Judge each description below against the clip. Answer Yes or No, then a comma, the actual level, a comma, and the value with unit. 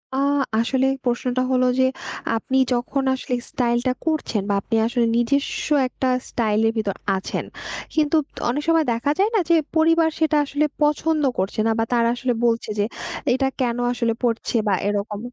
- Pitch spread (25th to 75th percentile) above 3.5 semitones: Yes, average, 4.0 semitones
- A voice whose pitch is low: No, very high, 250 Hz